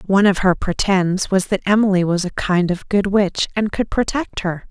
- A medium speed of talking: No, fast, 215 wpm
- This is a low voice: No, high, 190 Hz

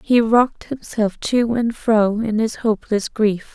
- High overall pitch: Yes, high, 220 Hz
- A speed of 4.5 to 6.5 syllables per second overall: No, 4.1 syllables/s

